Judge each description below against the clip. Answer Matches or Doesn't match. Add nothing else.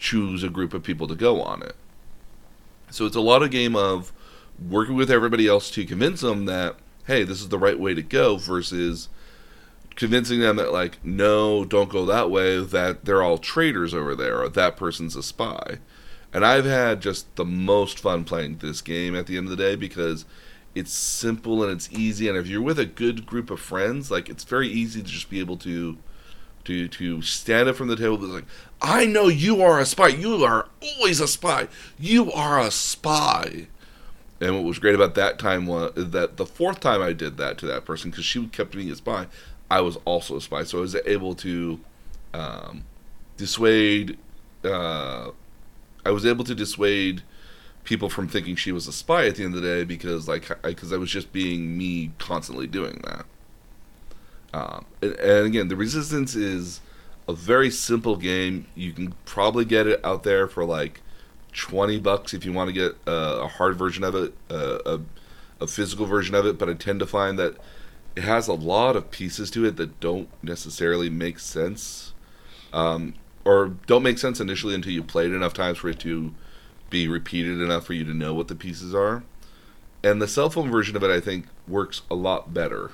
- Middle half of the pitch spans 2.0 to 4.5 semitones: Matches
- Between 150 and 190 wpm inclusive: Doesn't match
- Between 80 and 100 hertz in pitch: Matches